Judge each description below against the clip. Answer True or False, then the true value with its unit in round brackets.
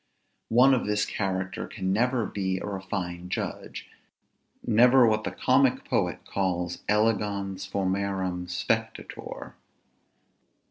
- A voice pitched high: False (100 Hz)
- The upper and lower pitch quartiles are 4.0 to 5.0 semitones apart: False (3.0 semitones)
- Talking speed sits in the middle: False (105 wpm)